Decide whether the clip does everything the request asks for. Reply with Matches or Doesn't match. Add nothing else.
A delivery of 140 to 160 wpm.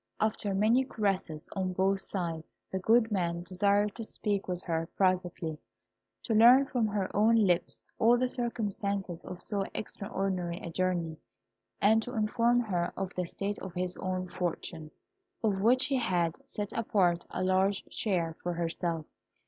Matches